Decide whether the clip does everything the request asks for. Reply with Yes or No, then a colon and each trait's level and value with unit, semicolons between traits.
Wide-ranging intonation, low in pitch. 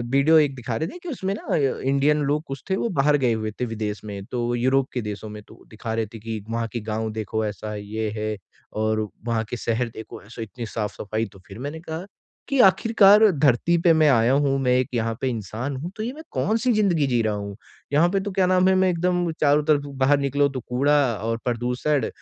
Yes: wide, 6.1 semitones; low, 130 Hz